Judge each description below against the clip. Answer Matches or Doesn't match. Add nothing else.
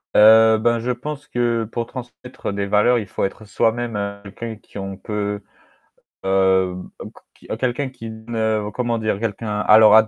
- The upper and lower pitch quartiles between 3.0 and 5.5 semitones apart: Doesn't match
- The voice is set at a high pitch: Doesn't match